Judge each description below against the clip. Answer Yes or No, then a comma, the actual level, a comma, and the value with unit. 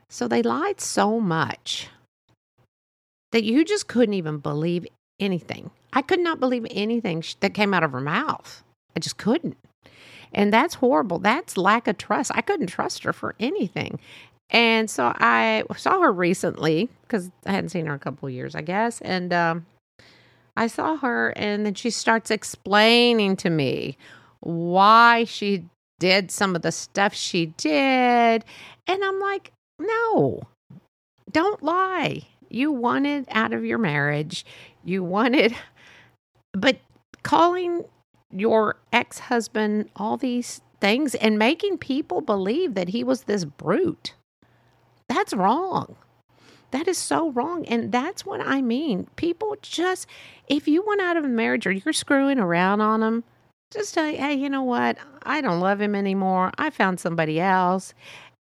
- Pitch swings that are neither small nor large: No, wide, 7.5 semitones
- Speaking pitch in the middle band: No, high, 225 Hz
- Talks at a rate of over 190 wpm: No, average, 155 wpm